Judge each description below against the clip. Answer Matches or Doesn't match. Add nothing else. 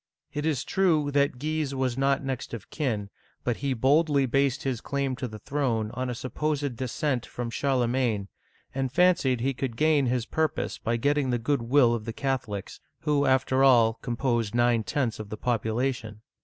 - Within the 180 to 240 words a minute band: Matches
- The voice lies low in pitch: Matches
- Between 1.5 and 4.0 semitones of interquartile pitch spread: Matches